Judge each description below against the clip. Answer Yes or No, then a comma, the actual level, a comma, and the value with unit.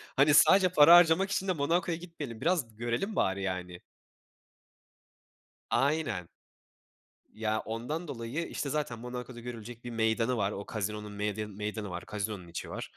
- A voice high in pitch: No, low, 120 Hz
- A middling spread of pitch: No, wide, 6.4 semitones